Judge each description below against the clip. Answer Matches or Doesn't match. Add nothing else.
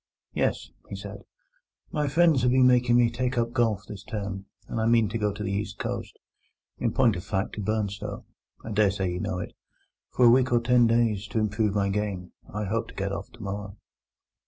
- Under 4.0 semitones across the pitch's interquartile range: Matches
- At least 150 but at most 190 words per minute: Doesn't match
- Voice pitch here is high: Doesn't match